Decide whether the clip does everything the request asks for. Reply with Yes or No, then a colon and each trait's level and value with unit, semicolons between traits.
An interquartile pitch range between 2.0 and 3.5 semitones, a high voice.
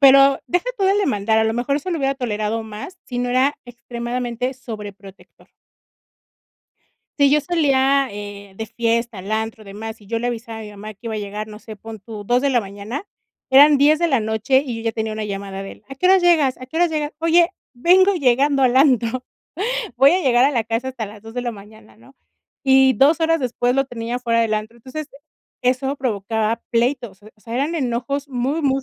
No: average, 4.0 semitones; high, 245 Hz